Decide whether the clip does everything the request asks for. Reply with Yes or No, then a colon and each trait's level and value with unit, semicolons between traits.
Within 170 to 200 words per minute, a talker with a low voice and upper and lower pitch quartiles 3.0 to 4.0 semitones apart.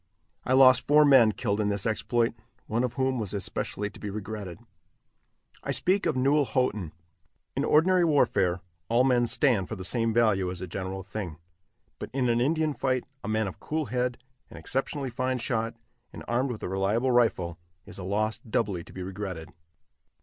No: average, 185 wpm; low, 115 Hz; average, 4.8 semitones